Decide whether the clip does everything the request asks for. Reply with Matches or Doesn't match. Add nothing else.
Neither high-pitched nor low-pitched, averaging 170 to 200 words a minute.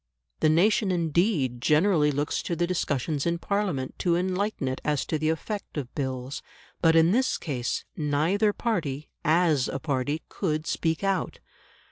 Doesn't match